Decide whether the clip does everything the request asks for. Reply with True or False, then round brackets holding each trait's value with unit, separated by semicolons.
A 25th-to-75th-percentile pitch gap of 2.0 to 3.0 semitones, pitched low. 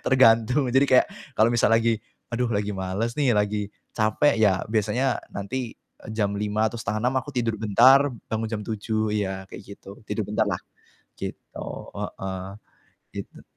True (2.5 semitones; 110 Hz)